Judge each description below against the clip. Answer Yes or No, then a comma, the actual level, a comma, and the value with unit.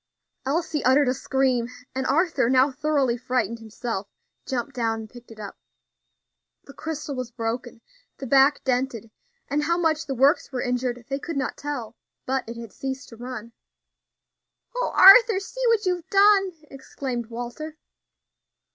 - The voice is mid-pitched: No, very high, 265 Hz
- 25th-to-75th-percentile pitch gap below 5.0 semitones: Yes, average, 4.0 semitones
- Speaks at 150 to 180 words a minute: Yes, average, 155 wpm